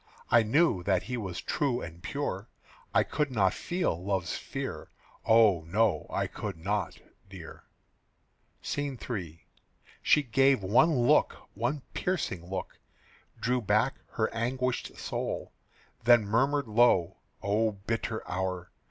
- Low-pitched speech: Yes, low, 110 Hz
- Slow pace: Yes, slow, 125 wpm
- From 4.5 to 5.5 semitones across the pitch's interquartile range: Yes, average, 5.2 semitones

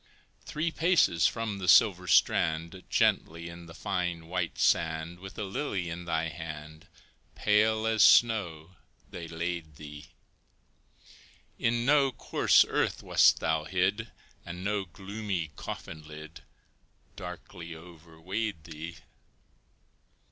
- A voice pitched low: Yes, very low, 85 Hz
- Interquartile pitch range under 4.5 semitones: Yes, average, 4.1 semitones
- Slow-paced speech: Yes, slow, 115 wpm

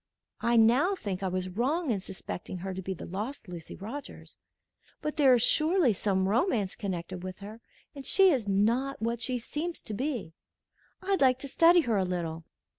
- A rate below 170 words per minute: No, average, 190 wpm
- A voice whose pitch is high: Yes, high, 225 Hz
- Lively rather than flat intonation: Yes, wide, 6.6 semitones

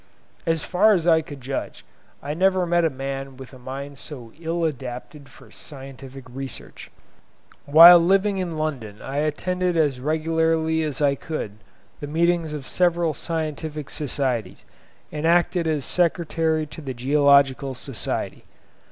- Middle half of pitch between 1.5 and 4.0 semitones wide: Yes, average, 3.4 semitones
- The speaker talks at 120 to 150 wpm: Yes, average, 145 wpm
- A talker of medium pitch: Yes, medium, 150 Hz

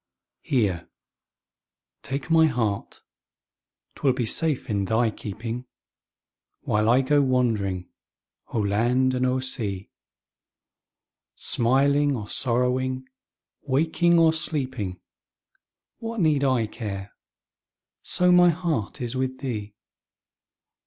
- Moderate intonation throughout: Yes, average, 4.5 semitones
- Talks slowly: Yes, slow, 100 wpm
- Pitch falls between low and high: No, low, 130 Hz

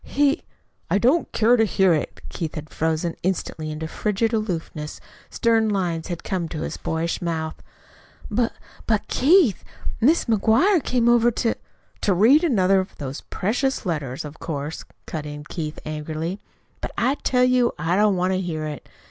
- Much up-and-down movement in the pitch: Yes, wide, 6.5 semitones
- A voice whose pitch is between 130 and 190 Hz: Yes, medium, 185 Hz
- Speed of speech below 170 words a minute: No, average, 175 wpm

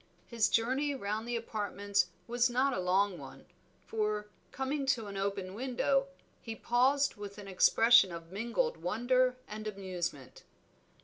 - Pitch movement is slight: No, average, 4.2 semitones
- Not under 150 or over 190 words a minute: No, average, 140 wpm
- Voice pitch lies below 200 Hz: No, high, 220 Hz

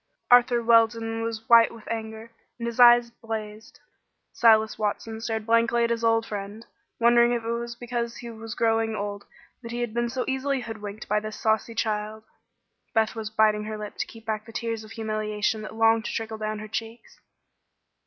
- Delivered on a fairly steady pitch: Yes, narrow, 1.3 semitones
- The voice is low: No, high, 225 Hz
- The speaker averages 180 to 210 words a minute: Yes, average, 190 wpm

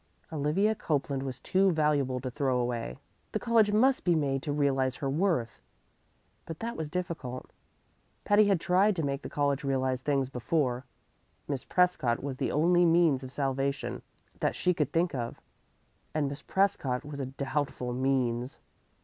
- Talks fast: No, average, 160 wpm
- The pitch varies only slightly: No, average, 4.6 semitones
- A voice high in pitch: No, medium, 140 Hz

